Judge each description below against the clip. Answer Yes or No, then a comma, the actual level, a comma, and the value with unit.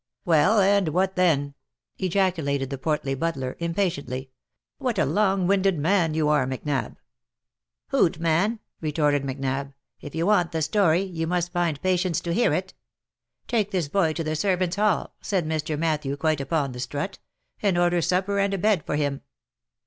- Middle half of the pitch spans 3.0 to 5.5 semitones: Yes, average, 4.6 semitones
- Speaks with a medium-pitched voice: Yes, medium, 165 Hz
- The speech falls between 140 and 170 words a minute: No, average, 190 wpm